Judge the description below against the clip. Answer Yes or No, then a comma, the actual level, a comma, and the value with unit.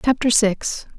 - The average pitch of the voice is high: Yes, high, 230 Hz